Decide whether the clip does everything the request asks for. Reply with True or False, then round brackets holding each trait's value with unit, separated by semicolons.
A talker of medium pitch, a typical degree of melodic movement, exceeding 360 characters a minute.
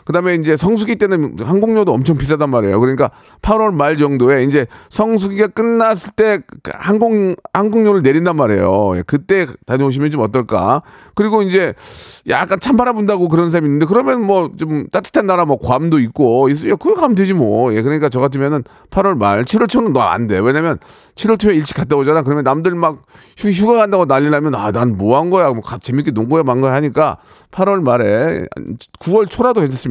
False (165 Hz; 7.1 semitones; 375 characters per minute)